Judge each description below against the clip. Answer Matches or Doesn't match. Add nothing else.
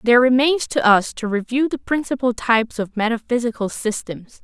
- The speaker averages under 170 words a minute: Matches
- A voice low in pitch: Doesn't match